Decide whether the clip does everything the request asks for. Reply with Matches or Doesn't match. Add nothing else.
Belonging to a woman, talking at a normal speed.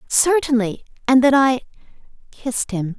Doesn't match